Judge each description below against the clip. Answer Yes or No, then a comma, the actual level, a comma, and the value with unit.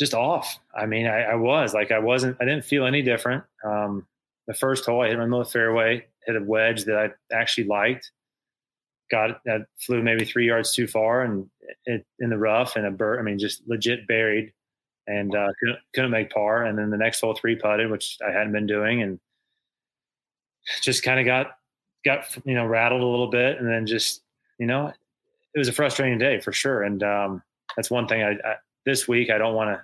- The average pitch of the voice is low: Yes, low, 115 Hz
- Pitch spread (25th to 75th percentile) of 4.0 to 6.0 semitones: No, narrow, 2.4 semitones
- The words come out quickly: Yes, fast, 215 wpm